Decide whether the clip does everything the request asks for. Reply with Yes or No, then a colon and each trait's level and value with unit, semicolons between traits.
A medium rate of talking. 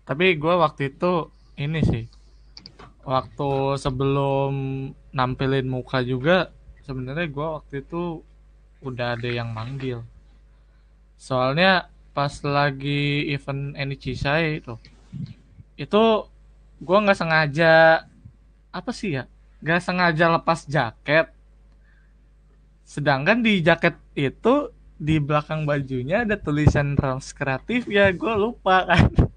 Yes: average, 105 wpm